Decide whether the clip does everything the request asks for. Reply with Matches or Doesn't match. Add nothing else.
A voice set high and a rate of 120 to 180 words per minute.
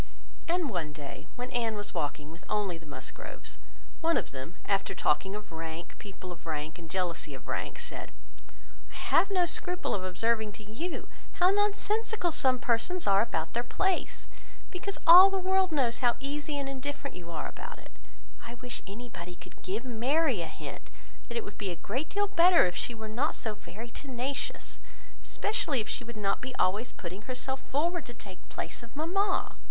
Doesn't match